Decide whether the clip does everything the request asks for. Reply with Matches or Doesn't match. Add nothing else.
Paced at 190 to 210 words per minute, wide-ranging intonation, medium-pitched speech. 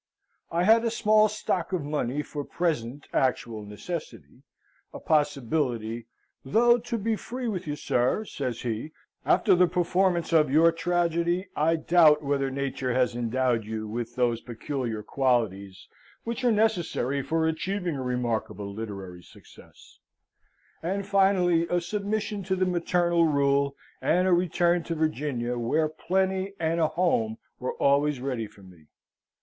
Doesn't match